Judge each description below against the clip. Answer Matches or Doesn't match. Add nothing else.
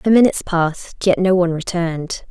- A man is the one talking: Doesn't match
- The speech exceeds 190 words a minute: Doesn't match